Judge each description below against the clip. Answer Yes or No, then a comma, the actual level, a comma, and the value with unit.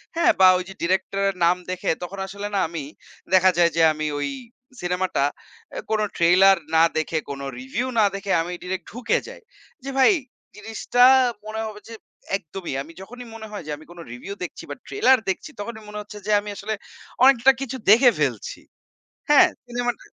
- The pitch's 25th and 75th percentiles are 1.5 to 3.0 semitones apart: No, average, 4.9 semitones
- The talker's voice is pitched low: No, high, 200 Hz